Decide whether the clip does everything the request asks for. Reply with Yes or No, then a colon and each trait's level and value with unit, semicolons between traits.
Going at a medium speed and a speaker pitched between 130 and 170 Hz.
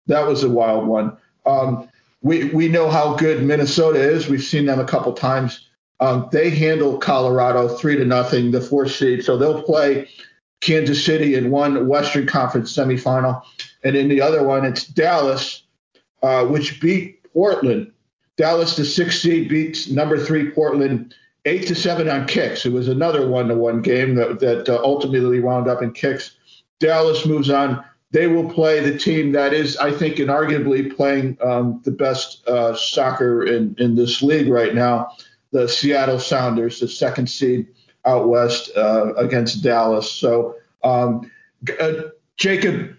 Yes: average, 165 wpm; low, 135 Hz